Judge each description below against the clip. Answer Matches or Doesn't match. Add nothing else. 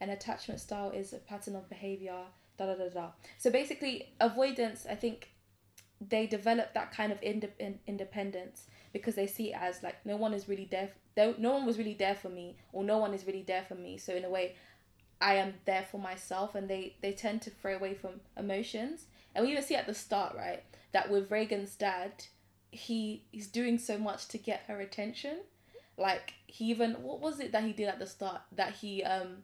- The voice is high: Matches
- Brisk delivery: Matches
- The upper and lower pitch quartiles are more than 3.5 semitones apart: Doesn't match